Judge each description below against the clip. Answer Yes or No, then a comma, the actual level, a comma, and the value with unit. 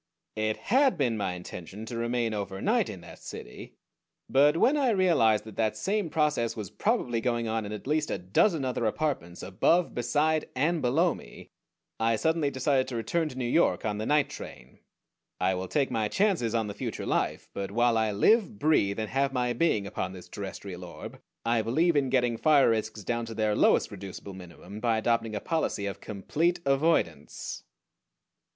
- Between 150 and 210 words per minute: Yes, average, 185 wpm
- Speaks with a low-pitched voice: Yes, low, 115 Hz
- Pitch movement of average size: No, wide, 6.1 semitones